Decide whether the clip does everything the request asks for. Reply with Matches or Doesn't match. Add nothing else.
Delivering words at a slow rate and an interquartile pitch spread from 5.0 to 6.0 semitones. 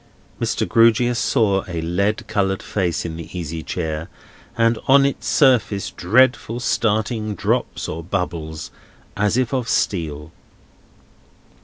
Matches